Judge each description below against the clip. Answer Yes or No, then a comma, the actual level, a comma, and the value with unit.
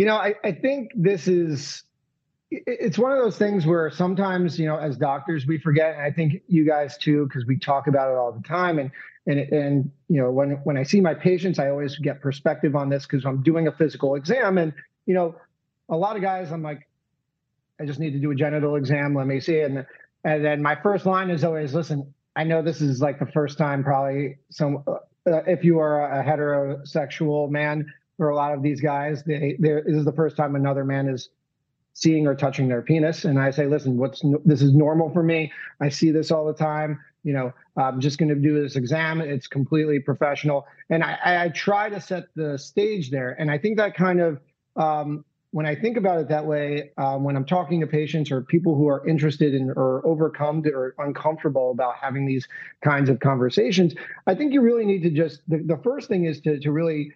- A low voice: No, medium, 150 Hz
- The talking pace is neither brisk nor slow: No, fast, 220 wpm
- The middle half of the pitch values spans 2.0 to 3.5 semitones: Yes, narrow, 2.6 semitones